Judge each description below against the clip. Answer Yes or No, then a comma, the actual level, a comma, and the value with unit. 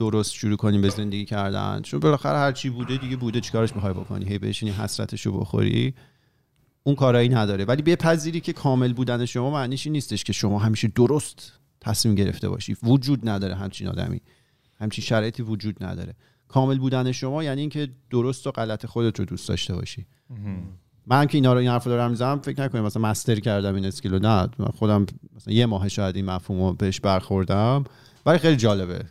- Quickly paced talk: Yes, fast, 175 wpm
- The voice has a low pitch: Yes, low, 115 Hz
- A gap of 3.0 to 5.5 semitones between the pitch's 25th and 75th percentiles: Yes, average, 4.4 semitones